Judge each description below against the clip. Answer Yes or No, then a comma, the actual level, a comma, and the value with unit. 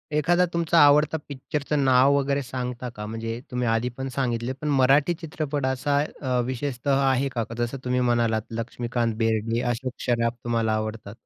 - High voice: No, low, 125 Hz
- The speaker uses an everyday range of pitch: Yes, average, 3.3 semitones